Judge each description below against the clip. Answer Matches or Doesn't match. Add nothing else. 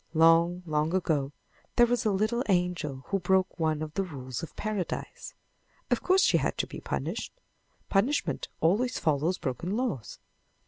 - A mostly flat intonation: Doesn't match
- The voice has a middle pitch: Matches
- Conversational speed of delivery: Matches